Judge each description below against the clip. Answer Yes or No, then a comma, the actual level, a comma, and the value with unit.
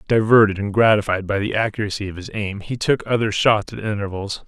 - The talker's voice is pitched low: Yes, low, 105 Hz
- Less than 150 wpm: No, average, 200 wpm